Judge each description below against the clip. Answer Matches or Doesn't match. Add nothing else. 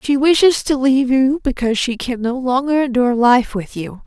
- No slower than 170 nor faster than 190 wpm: Doesn't match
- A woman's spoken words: Matches